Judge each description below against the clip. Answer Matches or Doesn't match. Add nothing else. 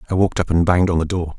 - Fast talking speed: Matches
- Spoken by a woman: Doesn't match